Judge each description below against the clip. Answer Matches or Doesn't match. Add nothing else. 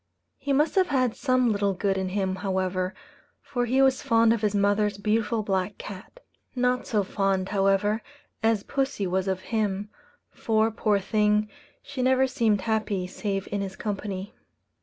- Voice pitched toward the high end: Matches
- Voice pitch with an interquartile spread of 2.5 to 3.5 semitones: Matches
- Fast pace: Doesn't match